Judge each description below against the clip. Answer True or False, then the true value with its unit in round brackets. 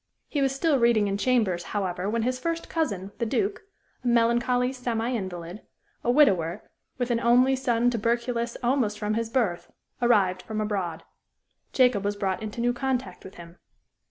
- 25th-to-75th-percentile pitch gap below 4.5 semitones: True (3.8 semitones)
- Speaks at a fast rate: False (165 wpm)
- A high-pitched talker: True (235 Hz)